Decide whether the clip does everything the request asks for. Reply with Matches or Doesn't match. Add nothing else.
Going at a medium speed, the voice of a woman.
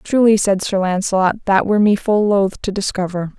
Matches